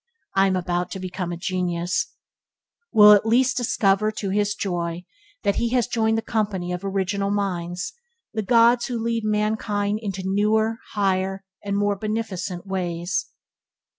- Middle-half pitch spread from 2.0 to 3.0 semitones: Yes, average, 2.7 semitones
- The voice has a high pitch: Yes, high, 200 Hz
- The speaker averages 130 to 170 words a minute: Yes, average, 150 wpm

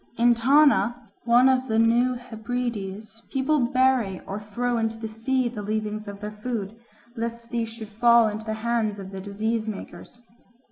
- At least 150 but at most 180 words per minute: Yes, average, 170 wpm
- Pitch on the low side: No, high, 225 Hz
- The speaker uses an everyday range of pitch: No, narrow, 2.3 semitones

